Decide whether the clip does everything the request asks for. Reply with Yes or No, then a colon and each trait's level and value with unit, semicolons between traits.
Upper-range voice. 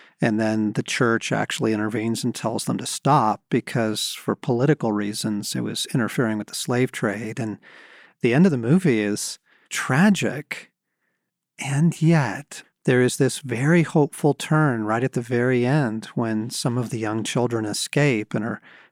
No: low, 120 Hz